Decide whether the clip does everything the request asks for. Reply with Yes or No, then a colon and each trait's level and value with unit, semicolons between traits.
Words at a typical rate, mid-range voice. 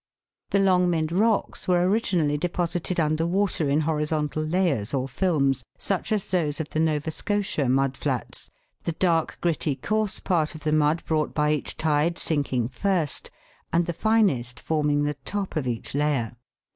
Yes: average, 160 wpm; medium, 155 Hz